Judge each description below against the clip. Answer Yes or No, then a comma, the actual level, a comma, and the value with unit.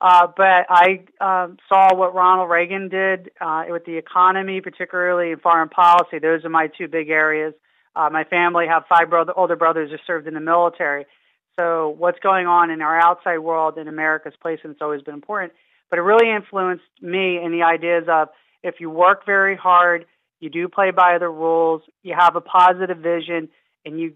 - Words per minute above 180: Yes, average, 195 wpm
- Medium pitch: Yes, medium, 170 Hz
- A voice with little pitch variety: Yes, narrow, 2.0 semitones